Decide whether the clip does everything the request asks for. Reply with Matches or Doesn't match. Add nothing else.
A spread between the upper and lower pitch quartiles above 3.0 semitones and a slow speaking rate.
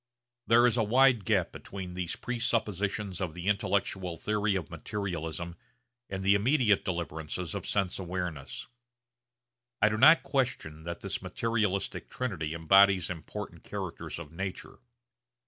Matches